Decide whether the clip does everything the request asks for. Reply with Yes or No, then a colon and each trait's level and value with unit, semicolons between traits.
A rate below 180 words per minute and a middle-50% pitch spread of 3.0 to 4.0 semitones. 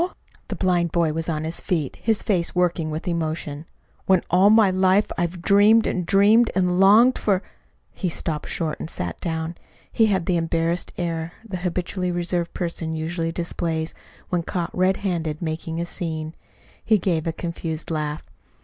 No: average, 170 wpm; narrow, 2.5 semitones